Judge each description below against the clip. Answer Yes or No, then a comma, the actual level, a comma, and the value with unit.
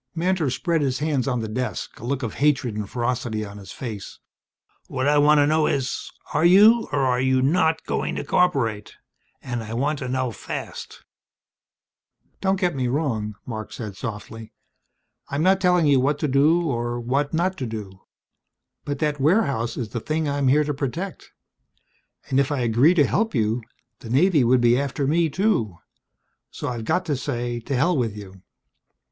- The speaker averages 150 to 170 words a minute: No, average, 190 wpm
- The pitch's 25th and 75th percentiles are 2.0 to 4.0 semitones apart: No, average, 4.6 semitones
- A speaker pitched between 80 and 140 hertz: Yes, low, 135 Hz